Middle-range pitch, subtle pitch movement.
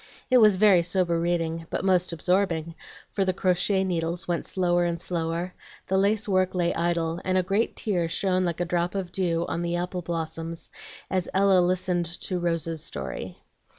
Yes: medium, 175 Hz; narrow, 1.9 semitones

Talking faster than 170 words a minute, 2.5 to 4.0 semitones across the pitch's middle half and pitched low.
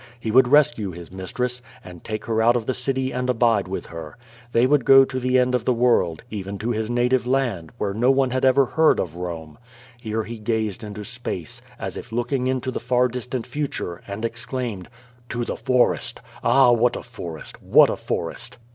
Yes: average, 200 wpm; average, 3.3 semitones; low, 120 Hz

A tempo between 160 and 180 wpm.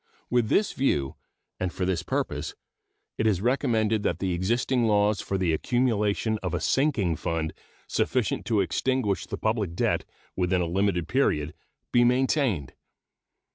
No: average, 145 wpm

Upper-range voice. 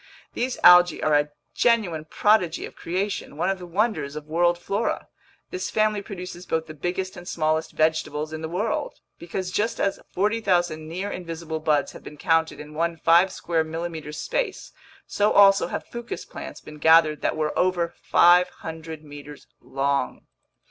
No: medium, 170 Hz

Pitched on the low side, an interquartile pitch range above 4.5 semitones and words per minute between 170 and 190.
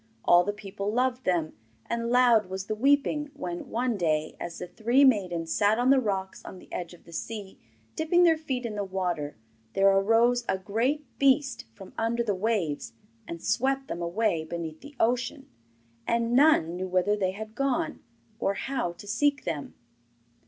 No: high, 215 Hz; wide, 5.5 semitones; average, 180 wpm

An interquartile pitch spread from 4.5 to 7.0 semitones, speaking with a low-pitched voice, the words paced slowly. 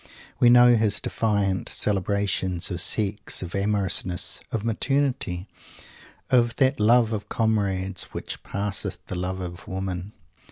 No: average, 3.3 semitones; low, 100 Hz; slow, 125 wpm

